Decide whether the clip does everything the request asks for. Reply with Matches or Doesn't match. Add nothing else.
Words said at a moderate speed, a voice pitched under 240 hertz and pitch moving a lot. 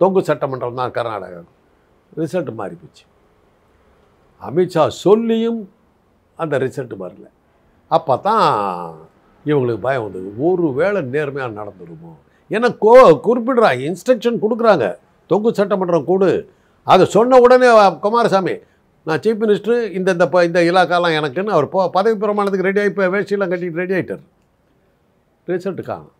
Matches